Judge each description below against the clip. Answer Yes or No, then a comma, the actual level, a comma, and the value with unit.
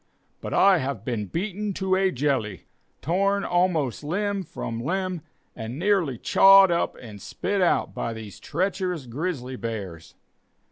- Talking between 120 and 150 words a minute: Yes, average, 140 wpm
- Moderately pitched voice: Yes, medium, 170 Hz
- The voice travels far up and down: Yes, wide, 8.0 semitones